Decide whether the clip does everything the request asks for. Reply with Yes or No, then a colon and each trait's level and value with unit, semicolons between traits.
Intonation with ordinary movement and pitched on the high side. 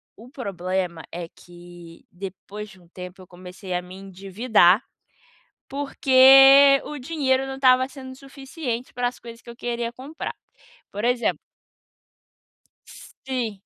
No: wide, 6.2 semitones; high, 235 Hz